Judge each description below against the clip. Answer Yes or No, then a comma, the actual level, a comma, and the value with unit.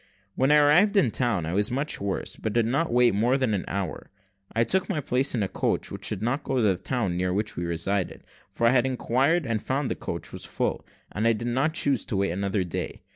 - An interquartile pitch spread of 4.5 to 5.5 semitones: Yes, average, 5.2 semitones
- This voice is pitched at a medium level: No, low, 115 Hz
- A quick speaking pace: Yes, fast, 245 wpm